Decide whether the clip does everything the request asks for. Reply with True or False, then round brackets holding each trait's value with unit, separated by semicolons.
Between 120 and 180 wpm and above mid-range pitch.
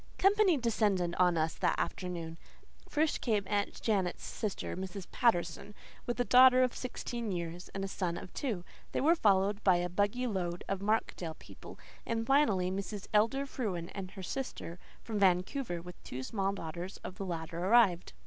True (170 wpm; 195 Hz)